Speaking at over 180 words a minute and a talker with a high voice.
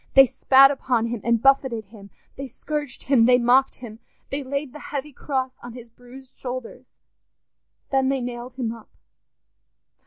No: average, 160 wpm; very high, 255 Hz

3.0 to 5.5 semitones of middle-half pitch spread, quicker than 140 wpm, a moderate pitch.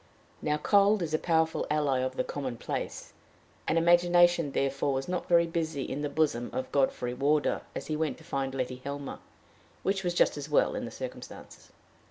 Yes: average, 3.8 semitones; average, 185 wpm; medium, 150 Hz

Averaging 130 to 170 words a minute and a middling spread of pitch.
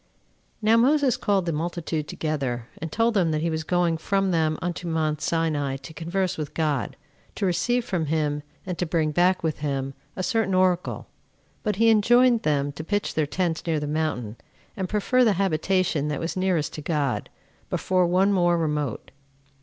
No: average, 185 wpm; average, 3.8 semitones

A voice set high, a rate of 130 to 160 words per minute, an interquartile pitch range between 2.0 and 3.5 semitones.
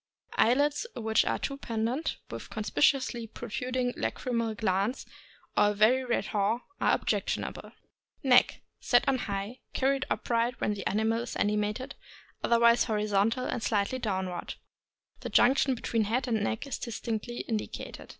Yes: high, 230 Hz; average, 150 wpm; average, 3.0 semitones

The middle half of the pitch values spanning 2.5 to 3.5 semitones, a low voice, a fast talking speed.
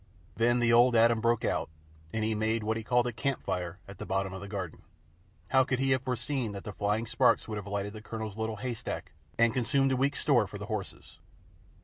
Yes: average, 2.8 semitones; low, 115 Hz; fast, 225 wpm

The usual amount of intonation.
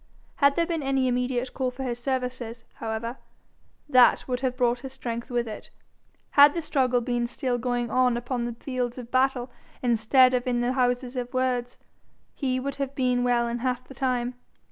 No: narrow, 1.3 semitones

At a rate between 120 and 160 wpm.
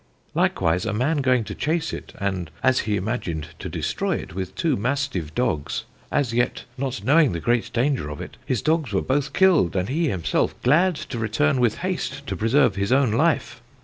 No: average, 195 wpm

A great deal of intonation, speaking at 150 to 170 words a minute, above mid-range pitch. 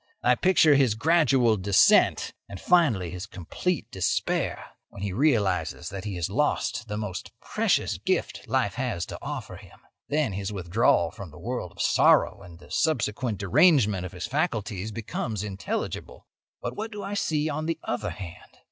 No: wide, 7.3 semitones; average, 165 wpm; low, 105 Hz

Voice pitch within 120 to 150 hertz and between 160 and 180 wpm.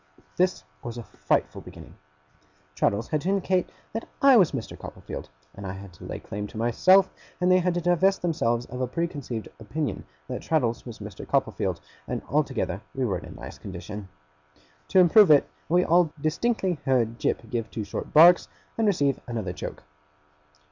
Yes: medium, 140 Hz; average, 175 wpm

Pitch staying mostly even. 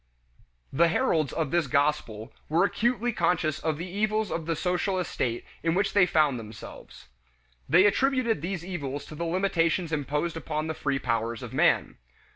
No: average, 4.1 semitones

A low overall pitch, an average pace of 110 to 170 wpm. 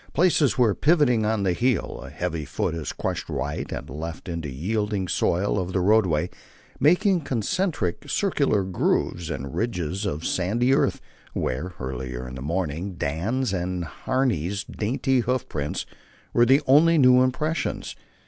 Yes: low, 100 Hz; average, 150 wpm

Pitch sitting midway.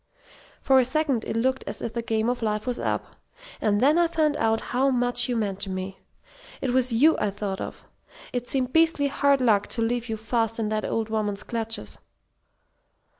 No: high, 235 Hz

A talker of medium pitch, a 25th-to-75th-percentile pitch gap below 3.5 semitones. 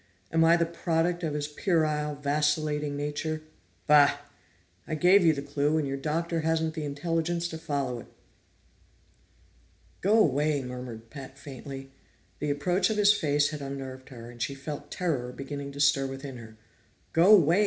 Yes: medium, 150 Hz; average, 2.9 semitones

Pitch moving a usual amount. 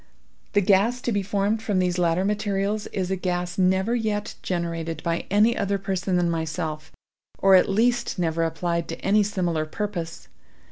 Yes: average, 3.3 semitones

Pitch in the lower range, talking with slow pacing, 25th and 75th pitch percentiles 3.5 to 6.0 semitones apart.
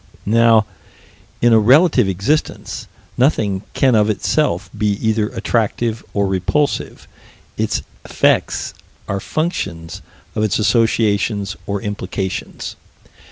No: low, 110 Hz; slow, 105 wpm; average, 2.8 semitones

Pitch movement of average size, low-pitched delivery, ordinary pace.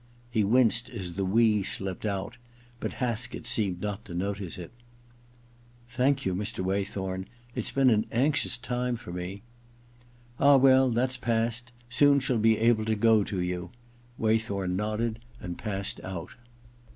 Yes: average, 3.8 semitones; low, 110 Hz; average, 155 wpm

